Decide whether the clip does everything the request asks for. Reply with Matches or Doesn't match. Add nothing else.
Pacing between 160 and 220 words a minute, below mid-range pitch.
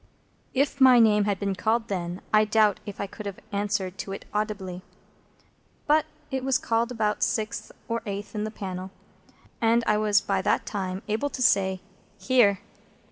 Doesn't match